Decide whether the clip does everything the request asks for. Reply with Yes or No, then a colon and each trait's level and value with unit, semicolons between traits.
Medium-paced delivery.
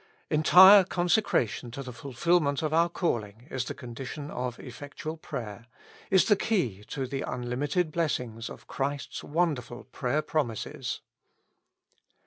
No: slow, 125 wpm